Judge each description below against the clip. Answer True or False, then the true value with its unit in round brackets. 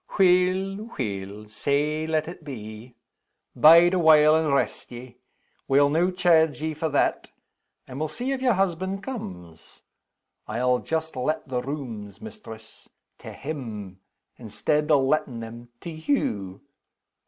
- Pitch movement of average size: False (6.2 semitones)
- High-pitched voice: False (150 Hz)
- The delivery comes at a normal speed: False (130 wpm)